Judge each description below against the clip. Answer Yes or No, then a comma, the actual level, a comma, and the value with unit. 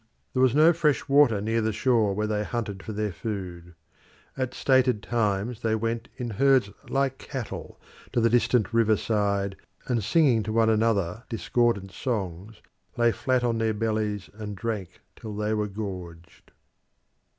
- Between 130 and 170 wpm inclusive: Yes, average, 160 wpm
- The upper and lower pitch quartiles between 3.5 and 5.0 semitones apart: No, average, 2.7 semitones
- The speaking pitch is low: Yes, low, 110 Hz